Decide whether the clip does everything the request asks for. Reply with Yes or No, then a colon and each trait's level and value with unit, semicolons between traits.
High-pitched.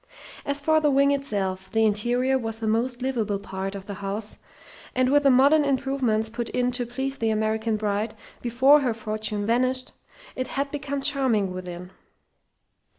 Yes: high, 235 Hz